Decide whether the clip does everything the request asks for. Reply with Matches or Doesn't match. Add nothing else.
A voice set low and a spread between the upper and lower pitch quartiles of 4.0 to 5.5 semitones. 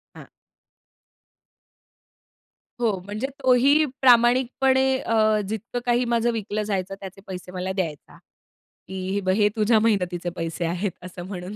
Doesn't match